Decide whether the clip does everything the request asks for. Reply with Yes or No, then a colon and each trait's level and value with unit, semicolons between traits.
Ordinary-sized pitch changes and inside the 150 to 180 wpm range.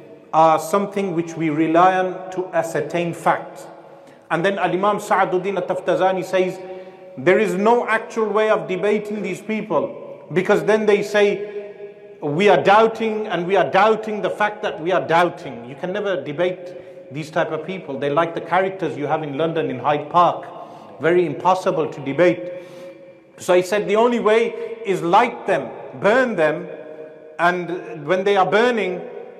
Yes: average, 3.5 semitones; average, 165 wpm